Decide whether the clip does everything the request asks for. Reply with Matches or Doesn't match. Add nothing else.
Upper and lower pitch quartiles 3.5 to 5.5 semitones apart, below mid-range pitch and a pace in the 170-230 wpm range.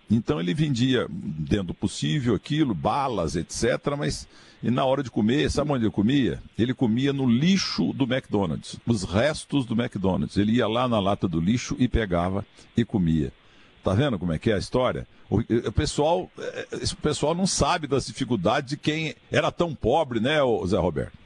Matches